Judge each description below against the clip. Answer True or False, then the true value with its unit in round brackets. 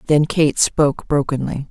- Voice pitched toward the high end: False (145 Hz)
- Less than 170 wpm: True (140 wpm)